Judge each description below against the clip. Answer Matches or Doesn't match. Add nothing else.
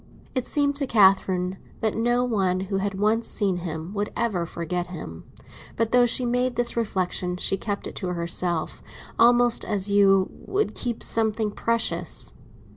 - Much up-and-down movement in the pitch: Doesn't match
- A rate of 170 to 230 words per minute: Doesn't match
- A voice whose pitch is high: Matches